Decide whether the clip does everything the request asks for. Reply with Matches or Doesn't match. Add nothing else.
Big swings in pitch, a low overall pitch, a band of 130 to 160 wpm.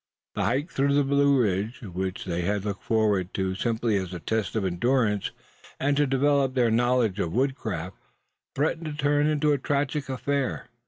Doesn't match